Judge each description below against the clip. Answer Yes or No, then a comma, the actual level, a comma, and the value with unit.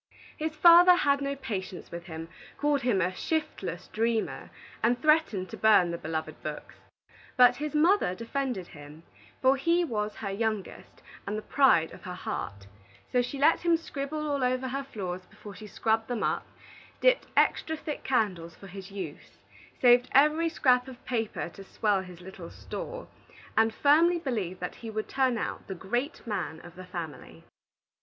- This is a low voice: No, high, 230 Hz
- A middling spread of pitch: No, wide, 7.2 semitones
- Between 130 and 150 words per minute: No, average, 170 wpm